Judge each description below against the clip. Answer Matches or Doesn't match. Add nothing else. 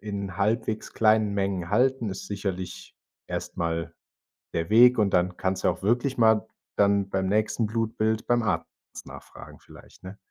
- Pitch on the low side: Matches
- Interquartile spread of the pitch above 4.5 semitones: Doesn't match